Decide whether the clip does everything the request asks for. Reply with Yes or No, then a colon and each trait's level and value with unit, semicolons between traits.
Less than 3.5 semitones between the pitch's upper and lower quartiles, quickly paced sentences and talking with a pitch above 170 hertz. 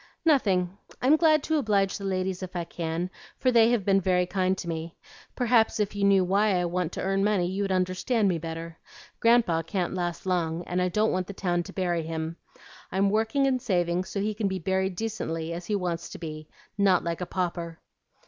Yes: average, 2.9 semitones; fast, 210 wpm; medium, 185 Hz